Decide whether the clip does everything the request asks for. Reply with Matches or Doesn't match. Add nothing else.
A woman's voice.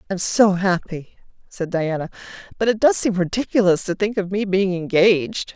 Matches